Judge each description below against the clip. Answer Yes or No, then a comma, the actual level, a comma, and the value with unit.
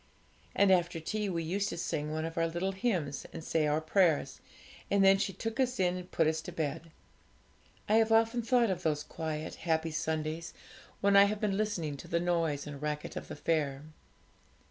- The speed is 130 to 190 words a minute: No, average, 200 wpm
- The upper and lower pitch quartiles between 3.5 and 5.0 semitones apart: Yes, average, 4.0 semitones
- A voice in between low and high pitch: Yes, medium, 170 Hz